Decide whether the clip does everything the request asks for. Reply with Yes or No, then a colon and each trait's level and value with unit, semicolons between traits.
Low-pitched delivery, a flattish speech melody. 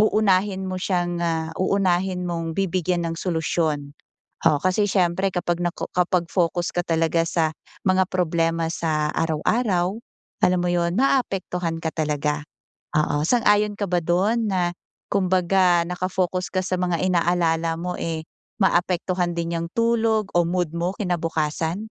No: medium, 175 Hz; narrow, 2.1 semitones